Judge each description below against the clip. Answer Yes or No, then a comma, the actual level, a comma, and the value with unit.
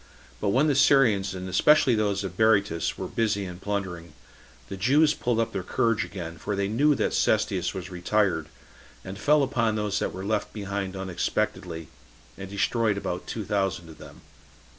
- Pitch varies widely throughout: No, average, 3.1 semitones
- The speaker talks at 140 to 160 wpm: No, average, 175 wpm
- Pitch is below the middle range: Yes, low, 100 Hz